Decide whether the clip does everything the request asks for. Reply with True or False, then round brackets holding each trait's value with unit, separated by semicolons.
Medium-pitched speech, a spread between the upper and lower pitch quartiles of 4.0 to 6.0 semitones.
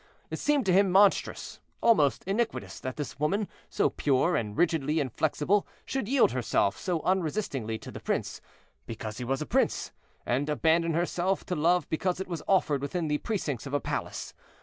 True (160 Hz; 5.4 semitones)